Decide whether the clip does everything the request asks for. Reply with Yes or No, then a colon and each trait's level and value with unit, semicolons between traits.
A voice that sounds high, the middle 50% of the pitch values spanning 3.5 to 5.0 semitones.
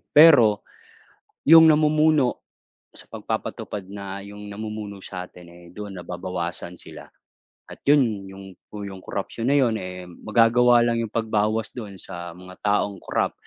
No: low, 105 Hz; average, 3.8 semitones